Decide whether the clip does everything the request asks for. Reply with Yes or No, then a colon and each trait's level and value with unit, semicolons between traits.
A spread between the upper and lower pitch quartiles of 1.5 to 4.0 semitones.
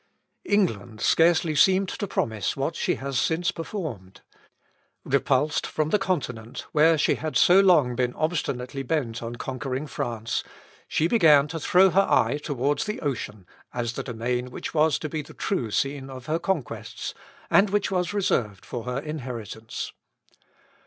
No: average, 5.3 semitones